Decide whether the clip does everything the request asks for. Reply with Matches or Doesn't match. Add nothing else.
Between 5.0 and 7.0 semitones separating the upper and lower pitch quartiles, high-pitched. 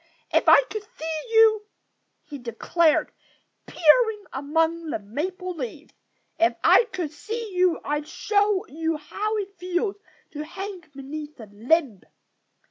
Matches